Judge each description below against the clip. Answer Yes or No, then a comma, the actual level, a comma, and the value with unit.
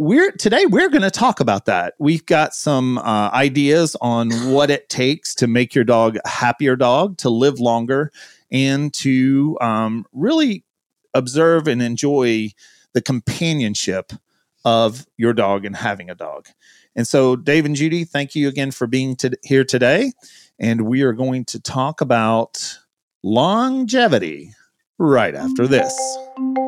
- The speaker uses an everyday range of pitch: Yes, average, 5.0 semitones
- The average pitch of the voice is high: No, low, 135 Hz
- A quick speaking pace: No, average, 150 wpm